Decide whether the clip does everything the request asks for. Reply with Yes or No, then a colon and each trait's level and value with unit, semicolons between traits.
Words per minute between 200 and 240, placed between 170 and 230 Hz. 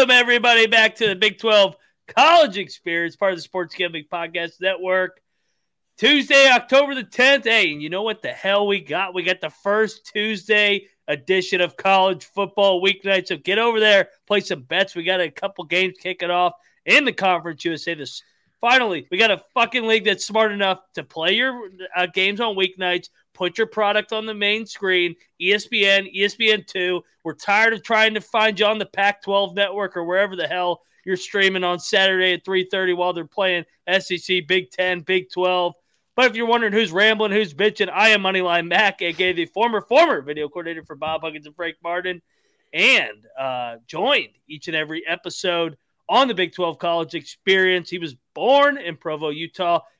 No: average, 190 wpm; high, 190 Hz